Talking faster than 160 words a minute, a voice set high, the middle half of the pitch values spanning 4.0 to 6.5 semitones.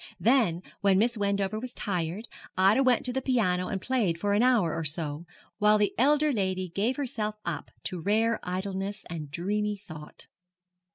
Yes: average, 170 wpm; high, 200 Hz; average, 4.3 semitones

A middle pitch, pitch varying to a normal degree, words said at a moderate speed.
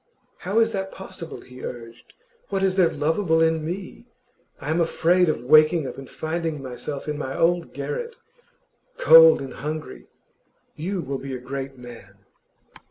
Yes: medium, 155 Hz; average, 4.9 semitones; average, 160 wpm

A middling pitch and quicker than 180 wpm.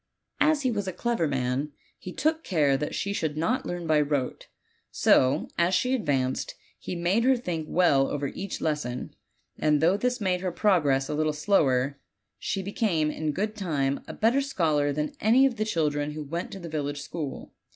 Yes: medium, 160 Hz; average, 190 wpm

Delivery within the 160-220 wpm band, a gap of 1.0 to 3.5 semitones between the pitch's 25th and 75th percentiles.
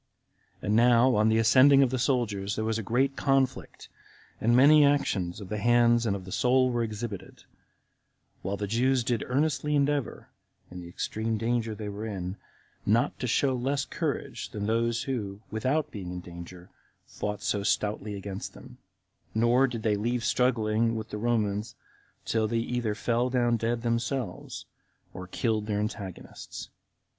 Yes: average, 165 wpm; average, 3.0 semitones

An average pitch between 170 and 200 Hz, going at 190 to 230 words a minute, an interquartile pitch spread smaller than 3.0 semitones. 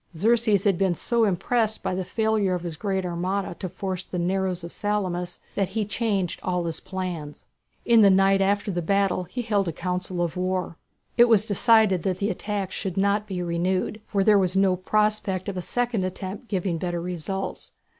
Yes: high, 190 Hz; average, 195 wpm; narrow, 2.4 semitones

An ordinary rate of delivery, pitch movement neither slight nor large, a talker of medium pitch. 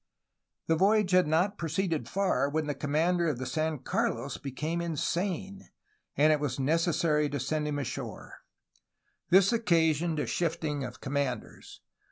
Yes: average, 145 wpm; average, 3.4 semitones; medium, 155 Hz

